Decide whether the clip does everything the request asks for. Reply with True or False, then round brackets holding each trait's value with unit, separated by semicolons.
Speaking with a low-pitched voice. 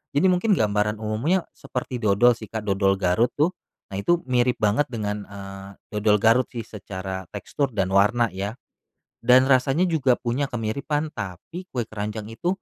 True (110 Hz)